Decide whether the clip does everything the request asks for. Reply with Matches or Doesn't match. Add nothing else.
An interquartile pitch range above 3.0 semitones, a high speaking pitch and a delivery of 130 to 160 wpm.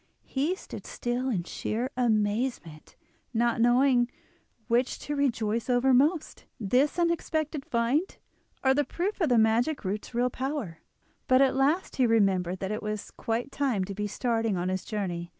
Matches